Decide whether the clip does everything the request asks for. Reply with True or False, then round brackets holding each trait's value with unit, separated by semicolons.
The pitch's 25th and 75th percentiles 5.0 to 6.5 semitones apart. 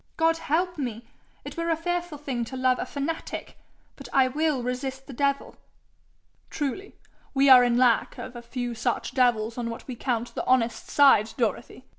False (3.4 semitones)